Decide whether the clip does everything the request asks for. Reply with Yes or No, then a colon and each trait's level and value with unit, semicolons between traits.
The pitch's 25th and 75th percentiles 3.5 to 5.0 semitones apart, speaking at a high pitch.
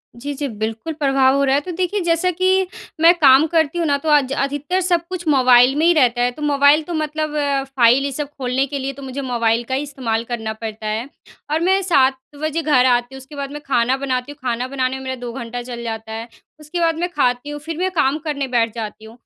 Yes: average, 3.8 semitones; very high, 275 Hz